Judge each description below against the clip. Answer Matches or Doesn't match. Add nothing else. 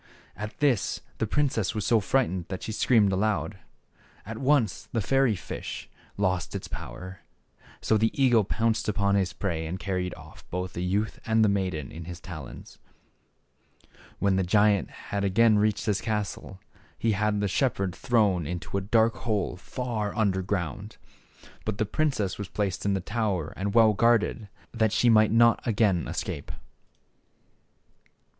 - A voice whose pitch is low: Matches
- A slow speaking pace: Doesn't match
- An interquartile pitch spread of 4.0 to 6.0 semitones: Doesn't match